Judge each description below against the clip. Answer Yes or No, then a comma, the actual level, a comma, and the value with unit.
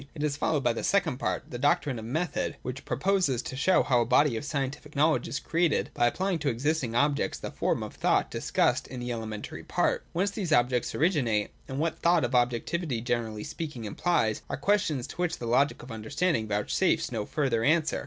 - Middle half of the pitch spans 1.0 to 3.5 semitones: No, average, 5.1 semitones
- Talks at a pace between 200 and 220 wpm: Yes, fast, 205 wpm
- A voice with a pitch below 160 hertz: Yes, medium, 140 Hz